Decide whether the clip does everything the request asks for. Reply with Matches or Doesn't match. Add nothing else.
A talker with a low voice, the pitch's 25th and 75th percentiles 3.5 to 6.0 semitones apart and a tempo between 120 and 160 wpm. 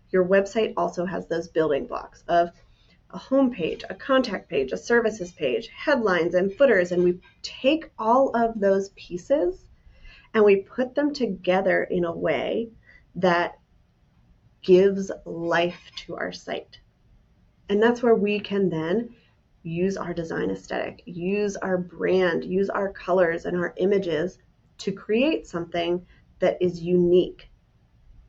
Doesn't match